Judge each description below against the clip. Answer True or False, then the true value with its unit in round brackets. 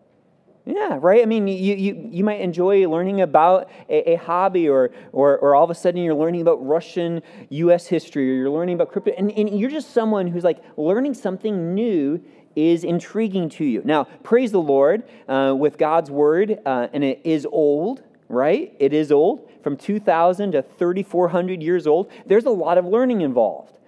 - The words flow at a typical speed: True (190 wpm)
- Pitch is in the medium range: True (175 Hz)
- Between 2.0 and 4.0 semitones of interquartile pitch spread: False (4.4 semitones)